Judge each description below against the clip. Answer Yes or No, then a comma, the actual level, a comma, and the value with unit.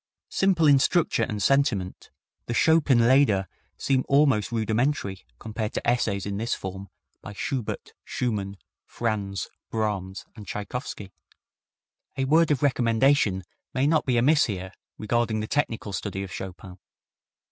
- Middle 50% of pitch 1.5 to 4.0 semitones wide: No, wide, 5.4 semitones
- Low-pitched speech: Yes, low, 115 Hz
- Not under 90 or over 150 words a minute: Yes, slow, 135 wpm